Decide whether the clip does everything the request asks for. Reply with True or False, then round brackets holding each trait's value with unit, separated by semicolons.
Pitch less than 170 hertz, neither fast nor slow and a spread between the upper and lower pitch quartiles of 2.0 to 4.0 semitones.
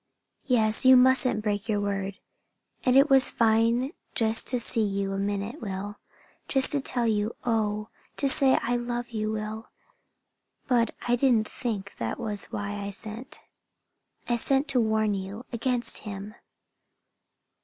False (220 Hz; 150 wpm; 3.1 semitones)